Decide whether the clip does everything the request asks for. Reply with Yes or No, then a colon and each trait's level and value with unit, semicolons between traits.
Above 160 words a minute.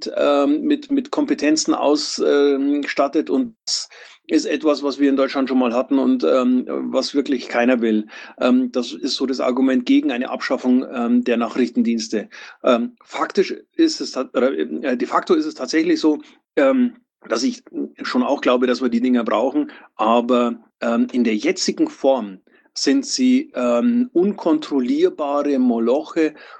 No: average, 155 wpm